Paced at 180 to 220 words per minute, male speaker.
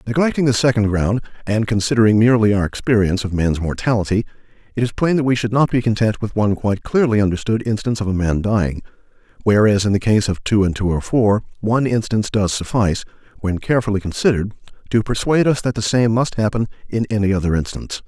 Yes: average, 200 wpm; male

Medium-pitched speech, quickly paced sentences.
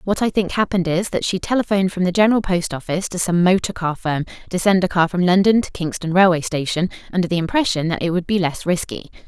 Yes: medium, 180 Hz; fast, 240 wpm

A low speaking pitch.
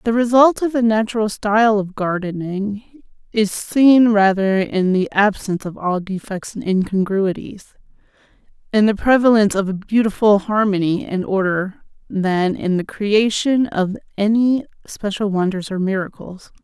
No: high, 205 Hz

